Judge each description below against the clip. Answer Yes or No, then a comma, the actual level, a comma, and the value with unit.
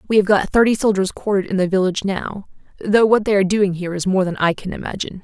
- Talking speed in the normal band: No, fast, 250 wpm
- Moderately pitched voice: No, high, 195 Hz